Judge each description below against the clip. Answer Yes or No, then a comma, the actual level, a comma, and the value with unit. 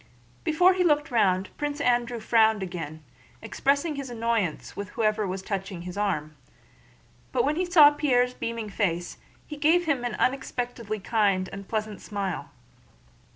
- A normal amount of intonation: No, wide, 6.3 semitones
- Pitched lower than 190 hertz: No, high, 225 Hz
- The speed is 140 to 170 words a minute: Yes, average, 150 wpm